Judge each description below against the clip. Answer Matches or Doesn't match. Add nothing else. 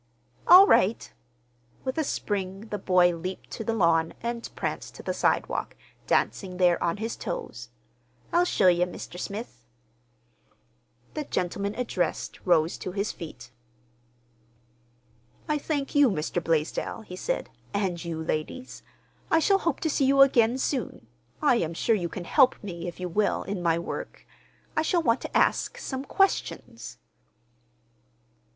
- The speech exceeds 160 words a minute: Doesn't match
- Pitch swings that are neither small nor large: Doesn't match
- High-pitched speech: Matches